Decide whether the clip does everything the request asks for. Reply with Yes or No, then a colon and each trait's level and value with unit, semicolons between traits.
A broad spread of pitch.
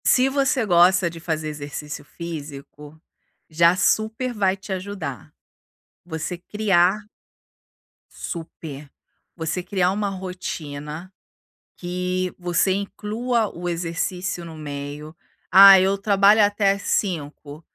No: average, 3.9 semitones